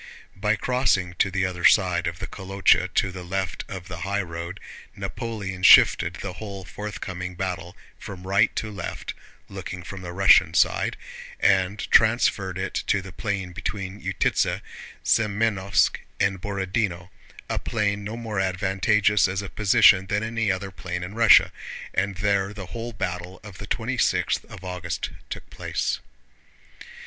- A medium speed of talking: Yes, average, 145 wpm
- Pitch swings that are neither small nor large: No, narrow, 2.1 semitones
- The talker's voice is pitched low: Yes, very low, 95 Hz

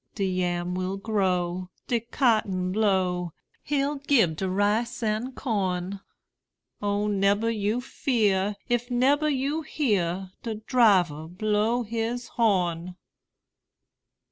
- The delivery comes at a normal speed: No, slow, 110 wpm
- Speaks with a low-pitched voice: No, high, 205 Hz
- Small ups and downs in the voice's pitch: No, average, 4.5 semitones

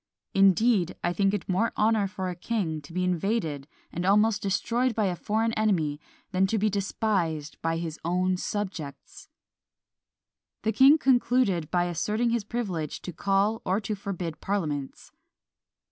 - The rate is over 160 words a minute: No, average, 150 wpm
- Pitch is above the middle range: Yes, high, 195 Hz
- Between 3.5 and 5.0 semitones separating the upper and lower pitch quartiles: Yes, average, 3.9 semitones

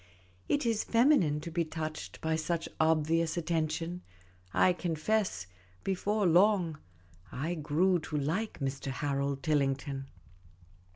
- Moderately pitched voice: Yes, medium, 160 Hz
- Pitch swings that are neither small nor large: Yes, average, 3.4 semitones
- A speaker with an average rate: No, slow, 115 wpm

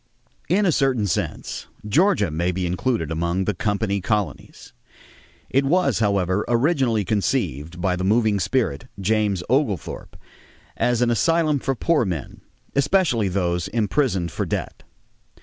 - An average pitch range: No, wide, 6.5 semitones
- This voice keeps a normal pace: No, slow, 130 wpm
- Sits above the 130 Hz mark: No, low, 105 Hz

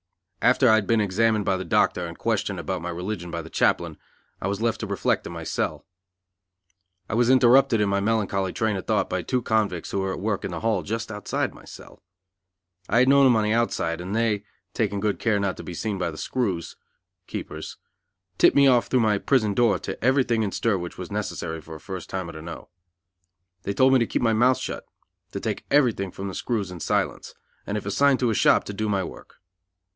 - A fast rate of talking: Yes, fast, 225 wpm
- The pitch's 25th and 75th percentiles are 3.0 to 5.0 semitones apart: Yes, average, 3.5 semitones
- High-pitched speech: No, low, 105 Hz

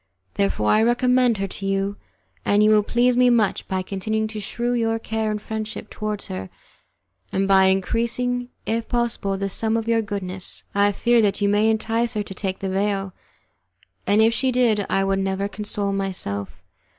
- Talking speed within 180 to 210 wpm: Yes, average, 185 wpm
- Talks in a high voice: Yes, high, 210 Hz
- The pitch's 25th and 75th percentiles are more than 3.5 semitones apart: No, average, 2.7 semitones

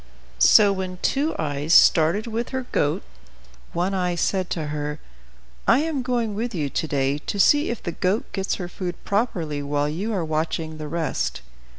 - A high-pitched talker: No, medium, 180 Hz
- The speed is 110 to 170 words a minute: No, average, 180 wpm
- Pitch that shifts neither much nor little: No, wide, 5.7 semitones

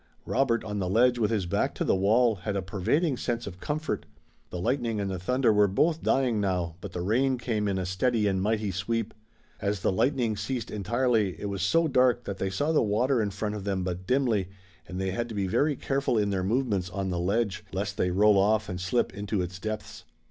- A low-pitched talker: Yes, low, 105 Hz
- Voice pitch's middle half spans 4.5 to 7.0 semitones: No, average, 3.8 semitones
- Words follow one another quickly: Yes, fast, 230 wpm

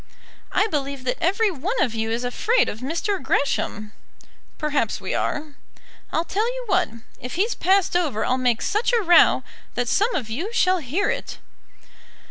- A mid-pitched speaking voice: No, very high, 315 Hz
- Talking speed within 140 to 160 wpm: No, average, 170 wpm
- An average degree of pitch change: No, wide, 8.2 semitones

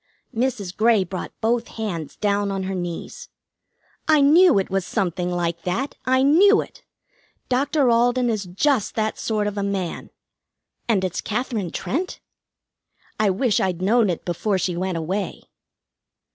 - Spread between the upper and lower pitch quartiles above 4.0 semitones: Yes, average, 5.0 semitones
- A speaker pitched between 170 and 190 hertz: No, high, 205 Hz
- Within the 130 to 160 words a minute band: Yes, average, 150 wpm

